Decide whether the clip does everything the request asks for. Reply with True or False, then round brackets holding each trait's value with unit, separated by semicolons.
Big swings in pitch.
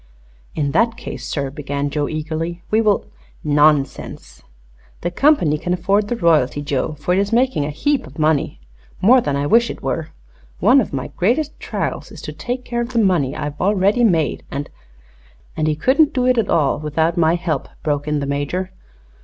True (6.9 semitones)